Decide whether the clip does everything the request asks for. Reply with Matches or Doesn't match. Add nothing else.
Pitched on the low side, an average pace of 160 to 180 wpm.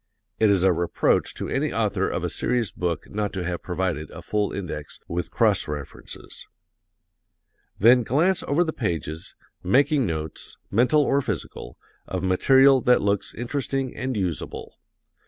Doesn't match